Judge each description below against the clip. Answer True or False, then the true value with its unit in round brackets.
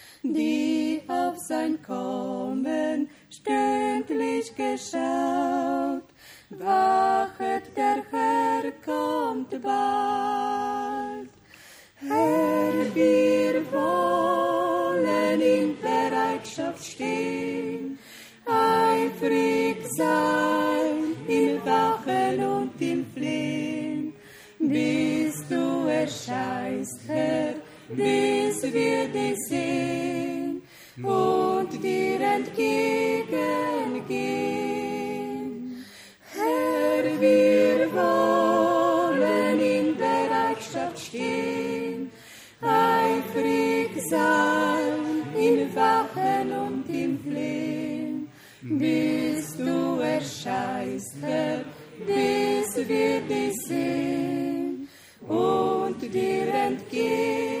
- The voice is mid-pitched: False (100 Hz)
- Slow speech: True (65 wpm)